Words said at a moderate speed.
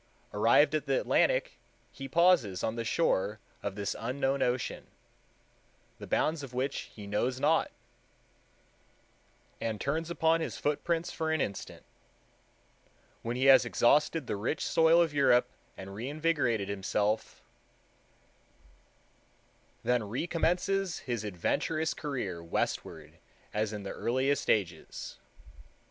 No: slow, 120 wpm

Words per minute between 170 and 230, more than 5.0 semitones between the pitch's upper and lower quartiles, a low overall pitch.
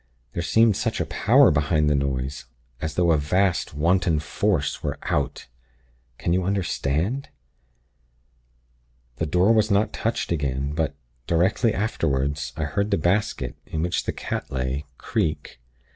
No: average, 145 wpm; wide, 5.5 semitones; very low, 85 Hz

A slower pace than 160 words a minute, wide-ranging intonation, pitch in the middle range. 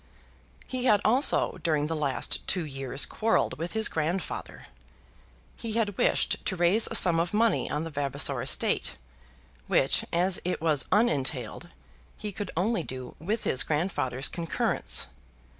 Yes: average, 145 wpm; wide, 5.9 semitones; medium, 170 Hz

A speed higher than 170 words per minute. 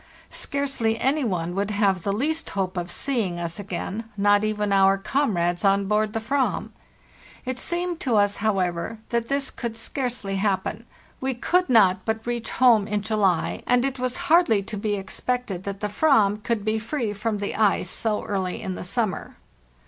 Yes: average, 180 wpm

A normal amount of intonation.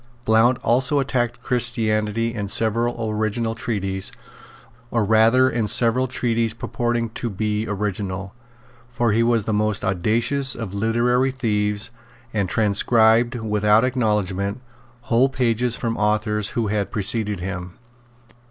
No: narrow, 2.3 semitones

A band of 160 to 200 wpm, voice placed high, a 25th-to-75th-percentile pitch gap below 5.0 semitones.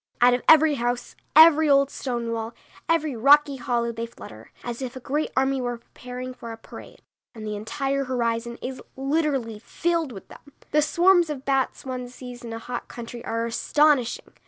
Yes: average, 180 wpm; very high, 250 Hz; average, 3.4 semitones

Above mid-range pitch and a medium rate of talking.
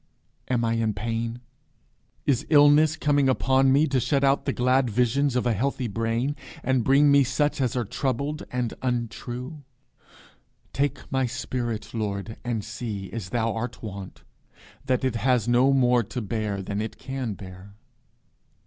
No: low, 125 Hz; average, 155 wpm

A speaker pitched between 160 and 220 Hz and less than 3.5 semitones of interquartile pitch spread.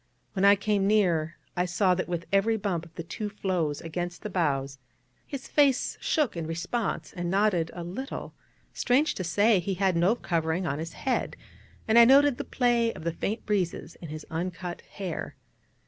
No: medium, 185 Hz; average, 4.3 semitones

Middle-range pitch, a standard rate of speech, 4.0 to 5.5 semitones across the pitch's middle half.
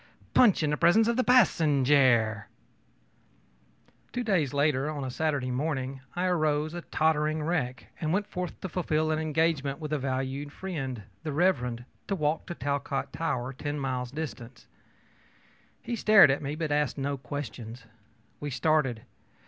No: medium, 150 Hz; average, 155 wpm; average, 3.5 semitones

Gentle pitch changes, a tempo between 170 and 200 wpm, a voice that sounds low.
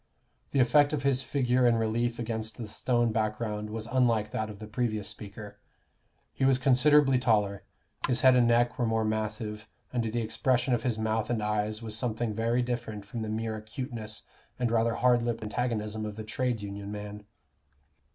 Yes: narrow, 2.3 semitones; average, 180 wpm; low, 115 Hz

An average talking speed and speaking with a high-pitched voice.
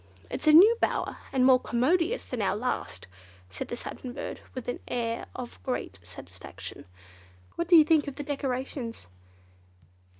Yes: average, 160 wpm; very high, 255 Hz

